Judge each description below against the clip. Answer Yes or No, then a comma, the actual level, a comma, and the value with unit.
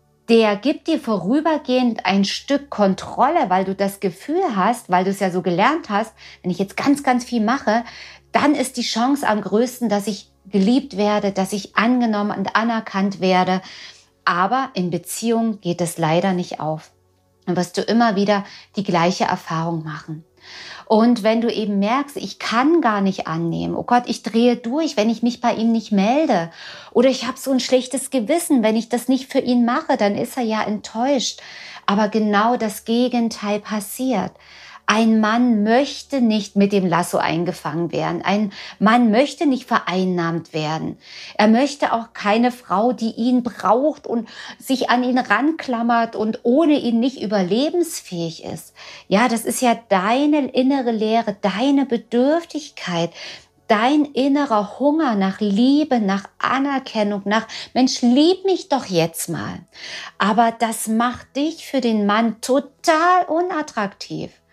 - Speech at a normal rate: Yes, average, 160 wpm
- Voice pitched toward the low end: No, high, 225 Hz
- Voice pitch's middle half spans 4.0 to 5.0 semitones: Yes, average, 4.3 semitones